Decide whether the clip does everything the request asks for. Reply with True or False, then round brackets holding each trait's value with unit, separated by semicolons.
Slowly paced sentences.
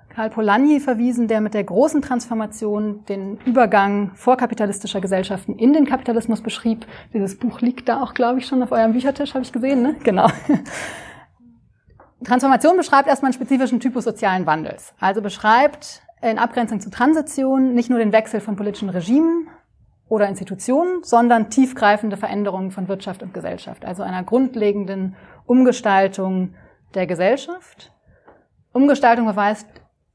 False (140 wpm)